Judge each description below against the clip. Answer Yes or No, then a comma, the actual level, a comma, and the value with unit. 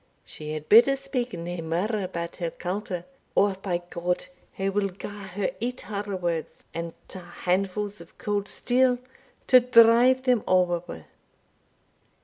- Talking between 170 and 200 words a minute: No, average, 145 wpm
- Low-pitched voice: No, high, 195 Hz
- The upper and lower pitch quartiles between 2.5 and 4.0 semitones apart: No, average, 4.7 semitones